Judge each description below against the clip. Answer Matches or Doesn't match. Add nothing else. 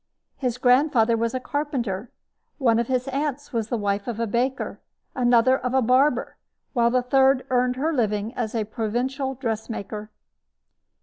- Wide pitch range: Doesn't match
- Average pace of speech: Matches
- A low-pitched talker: Doesn't match